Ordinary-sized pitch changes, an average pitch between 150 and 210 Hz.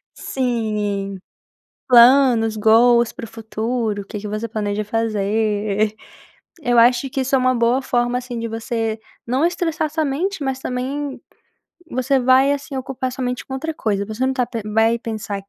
No: average, 3.2 semitones; high, 240 Hz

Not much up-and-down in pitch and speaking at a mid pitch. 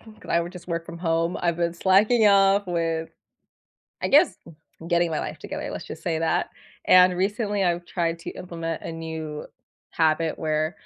Yes: narrow, 2.3 semitones; medium, 170 Hz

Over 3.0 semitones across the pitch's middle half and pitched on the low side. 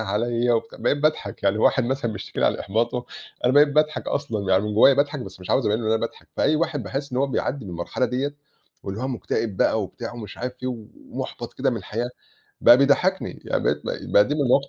Yes: average, 4.4 semitones; low, 120 Hz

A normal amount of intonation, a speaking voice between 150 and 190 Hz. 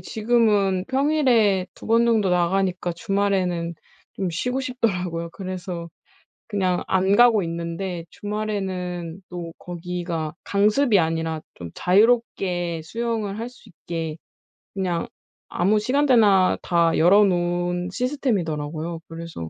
Yes: average, 3.9 semitones; medium, 185 Hz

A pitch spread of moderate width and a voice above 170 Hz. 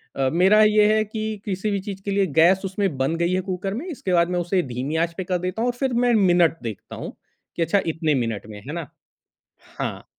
Yes: average, 4.0 semitones; medium, 185 Hz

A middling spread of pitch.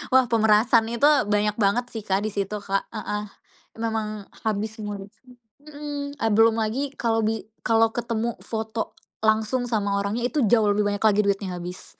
No: narrow, 2.0 semitones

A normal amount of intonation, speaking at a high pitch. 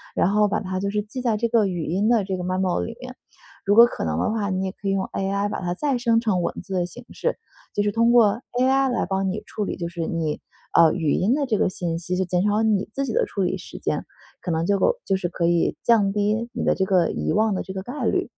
Yes: average, 3.8 semitones; high, 200 Hz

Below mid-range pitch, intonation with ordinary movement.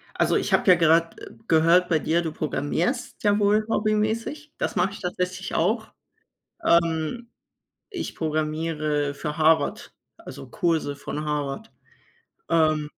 No: medium, 165 Hz; average, 4.8 semitones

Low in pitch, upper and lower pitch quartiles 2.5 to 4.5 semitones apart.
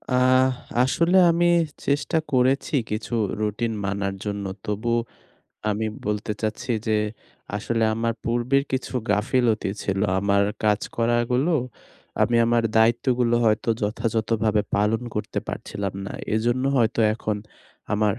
Yes: low, 115 Hz; average, 2.8 semitones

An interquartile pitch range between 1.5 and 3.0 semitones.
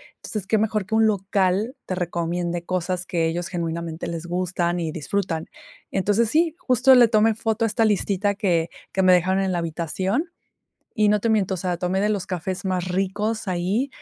No: average, 3.4 semitones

